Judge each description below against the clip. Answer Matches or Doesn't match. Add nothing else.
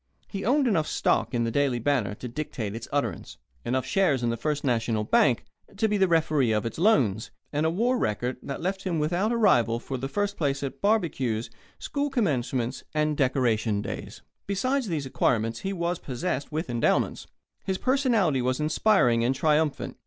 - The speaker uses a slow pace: Doesn't match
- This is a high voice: Doesn't match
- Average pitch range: Doesn't match